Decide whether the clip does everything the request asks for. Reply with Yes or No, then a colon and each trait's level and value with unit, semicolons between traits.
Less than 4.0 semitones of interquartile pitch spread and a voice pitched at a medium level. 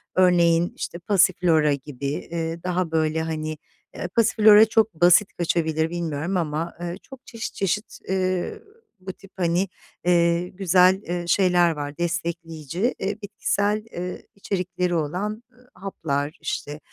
Yes: average, 2.9 semitones; medium, 175 Hz